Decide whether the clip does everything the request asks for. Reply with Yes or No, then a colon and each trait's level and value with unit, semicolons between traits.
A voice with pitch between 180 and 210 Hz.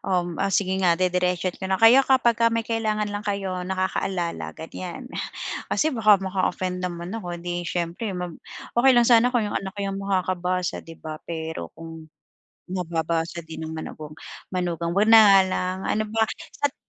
Yes: medium, 185 Hz